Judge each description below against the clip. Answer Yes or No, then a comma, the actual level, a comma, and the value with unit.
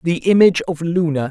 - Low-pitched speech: No, medium, 165 Hz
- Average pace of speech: Yes, average, 185 wpm